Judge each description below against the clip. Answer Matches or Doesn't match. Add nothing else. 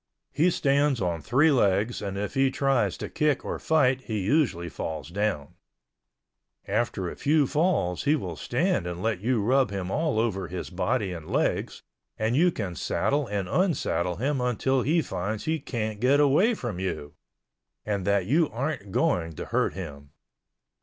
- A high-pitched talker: Doesn't match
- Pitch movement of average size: Doesn't match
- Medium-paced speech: Matches